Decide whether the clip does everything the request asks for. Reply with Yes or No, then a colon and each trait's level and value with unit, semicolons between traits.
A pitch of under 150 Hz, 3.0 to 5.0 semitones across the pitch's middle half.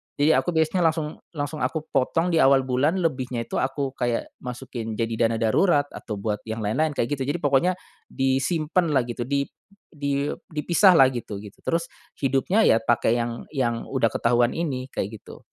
Yes: low, 135 Hz; average, 4.6 semitones